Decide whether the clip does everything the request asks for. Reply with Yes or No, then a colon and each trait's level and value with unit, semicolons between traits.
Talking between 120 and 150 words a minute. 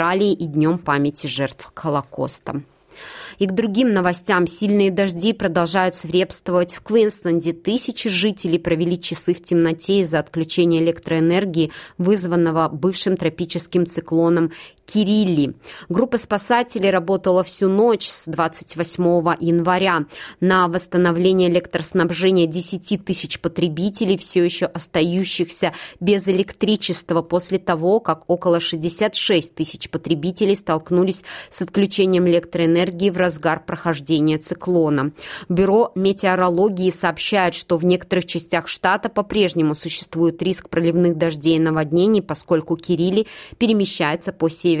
No: slow, 110 wpm